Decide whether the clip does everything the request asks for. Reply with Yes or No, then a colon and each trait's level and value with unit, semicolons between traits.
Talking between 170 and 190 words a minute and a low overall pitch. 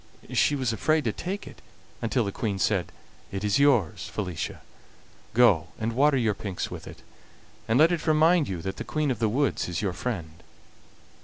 Yes: average, 185 wpm; low, 115 Hz